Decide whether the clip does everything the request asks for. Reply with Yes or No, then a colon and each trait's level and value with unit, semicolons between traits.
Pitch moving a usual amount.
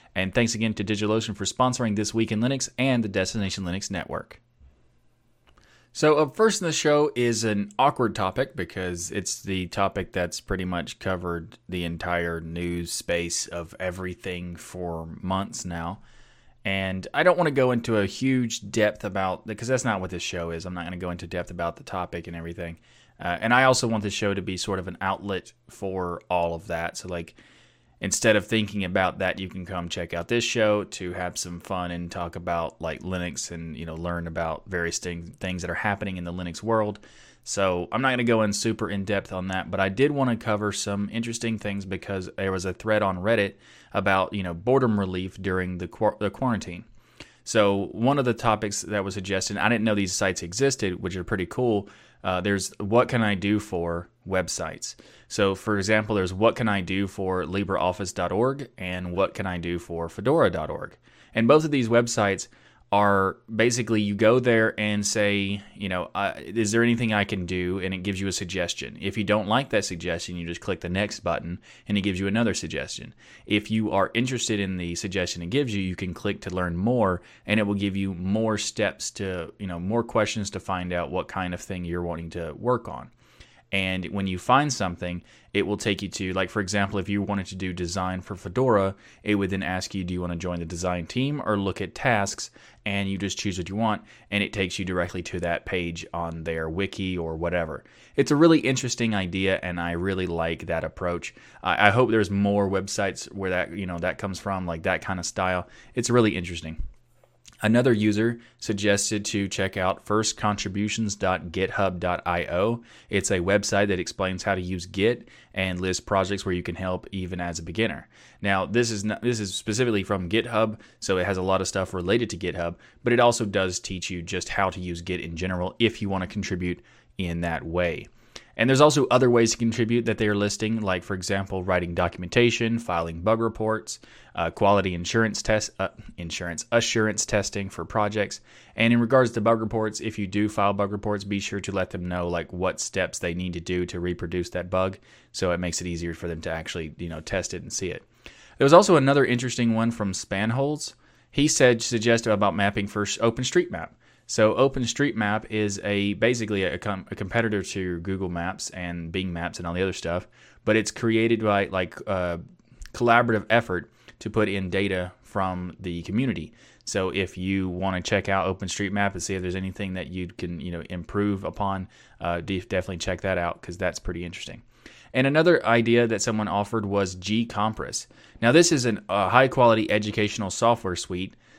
Yes: average, 3.6 semitones